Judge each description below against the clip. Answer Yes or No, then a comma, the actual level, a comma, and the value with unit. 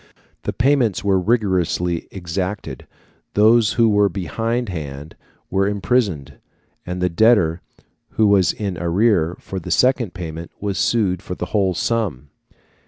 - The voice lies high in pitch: No, very low, 95 Hz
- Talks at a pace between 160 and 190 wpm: No, slow, 135 wpm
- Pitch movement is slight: No, average, 4.3 semitones